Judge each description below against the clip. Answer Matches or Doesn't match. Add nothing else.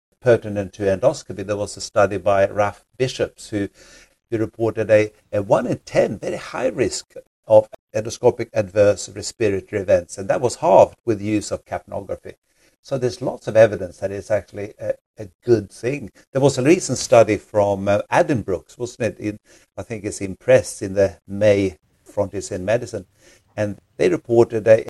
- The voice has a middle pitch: Doesn't match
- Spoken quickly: Doesn't match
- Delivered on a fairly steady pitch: Matches